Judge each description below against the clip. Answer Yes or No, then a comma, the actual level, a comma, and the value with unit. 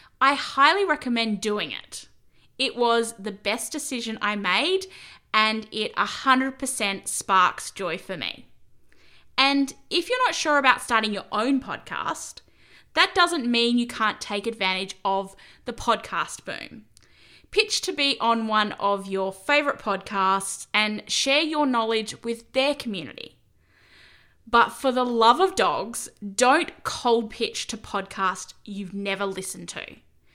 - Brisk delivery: No, average, 140 wpm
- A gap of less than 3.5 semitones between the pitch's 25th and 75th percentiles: No, average, 5.1 semitones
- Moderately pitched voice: No, high, 230 Hz